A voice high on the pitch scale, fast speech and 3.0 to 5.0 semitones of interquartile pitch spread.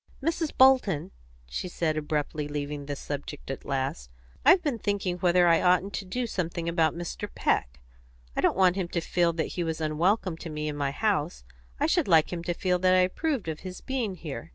No: medium, 175 Hz; fast, 210 wpm; average, 4.0 semitones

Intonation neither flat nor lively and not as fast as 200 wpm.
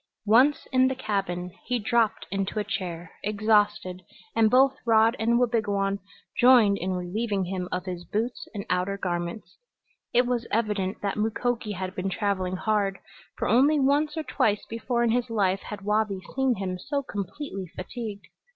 Yes: average, 3.9 semitones; average, 160 wpm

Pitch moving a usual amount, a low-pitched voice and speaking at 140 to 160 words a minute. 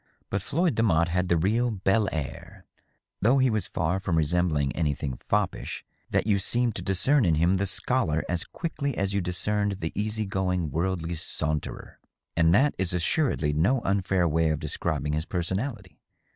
No: average, 4.4 semitones; very low, 95 Hz; average, 170 wpm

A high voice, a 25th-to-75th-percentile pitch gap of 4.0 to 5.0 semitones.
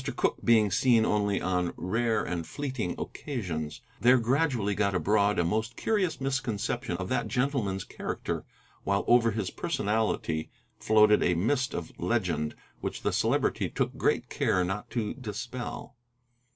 No: low, 110 Hz; average, 4.4 semitones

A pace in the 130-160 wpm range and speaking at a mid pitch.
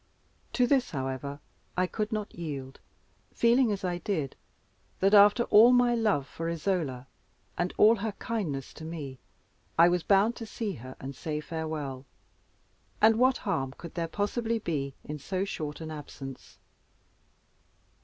Yes: average, 150 wpm; medium, 170 Hz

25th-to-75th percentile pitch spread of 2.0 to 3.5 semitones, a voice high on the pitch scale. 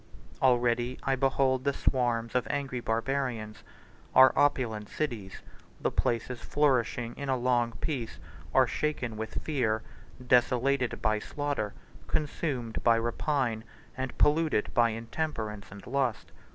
No: average, 3.2 semitones; low, 125 Hz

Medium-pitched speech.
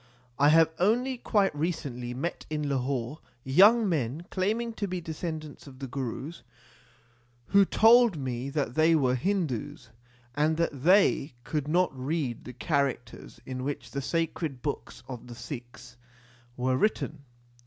Yes: medium, 150 Hz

